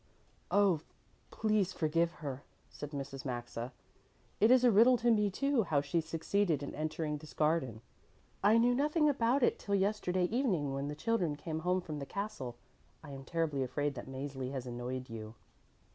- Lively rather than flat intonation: Yes, wide, 7.2 semitones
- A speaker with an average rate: Yes, average, 175 wpm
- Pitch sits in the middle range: Yes, medium, 160 Hz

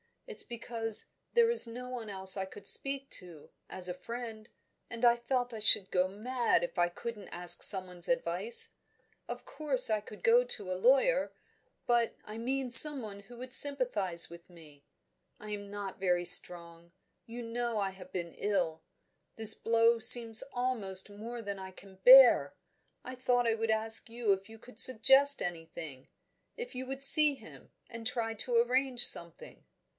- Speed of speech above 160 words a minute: Yes, average, 170 wpm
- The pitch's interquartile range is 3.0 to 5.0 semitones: Yes, average, 4.7 semitones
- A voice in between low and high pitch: No, high, 225 Hz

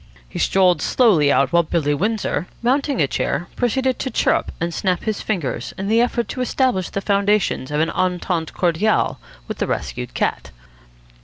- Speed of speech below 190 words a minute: Yes, average, 170 wpm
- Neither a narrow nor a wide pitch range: No, wide, 5.7 semitones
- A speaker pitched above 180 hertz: Yes, high, 190 Hz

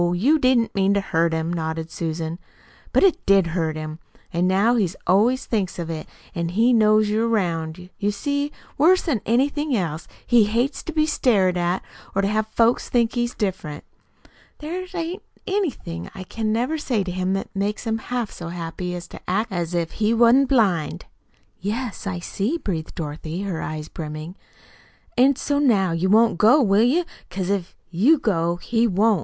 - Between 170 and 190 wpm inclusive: Yes, average, 180 wpm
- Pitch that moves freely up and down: Yes, wide, 5.7 semitones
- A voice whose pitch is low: No, high, 200 Hz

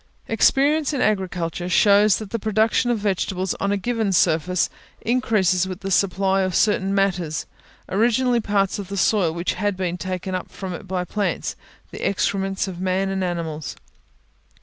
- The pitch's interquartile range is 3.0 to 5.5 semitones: No, narrow, 2.5 semitones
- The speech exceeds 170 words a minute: No, average, 165 wpm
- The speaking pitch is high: Yes, high, 195 Hz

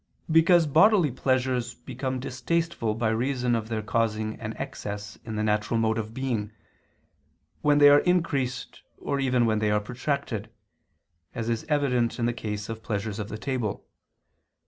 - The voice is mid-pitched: No, low, 120 Hz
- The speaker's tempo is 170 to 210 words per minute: No, average, 160 wpm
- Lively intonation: No, average, 3.9 semitones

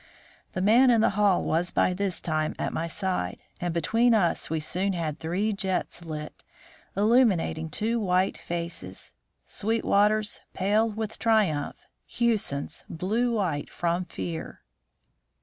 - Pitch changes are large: No, average, 4.7 semitones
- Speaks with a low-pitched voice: No, medium, 185 Hz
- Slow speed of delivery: Yes, slow, 130 wpm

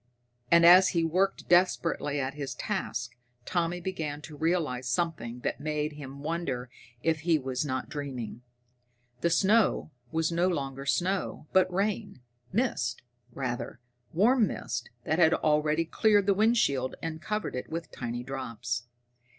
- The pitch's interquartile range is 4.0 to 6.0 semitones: Yes, average, 5.2 semitones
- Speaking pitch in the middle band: Yes, medium, 155 Hz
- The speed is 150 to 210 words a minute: No, average, 140 wpm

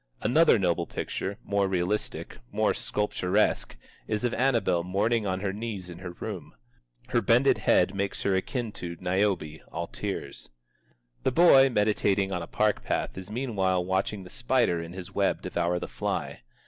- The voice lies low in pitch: Yes, low, 100 Hz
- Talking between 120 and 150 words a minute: No, average, 160 wpm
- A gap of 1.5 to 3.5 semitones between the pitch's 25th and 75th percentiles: Yes, average, 3.2 semitones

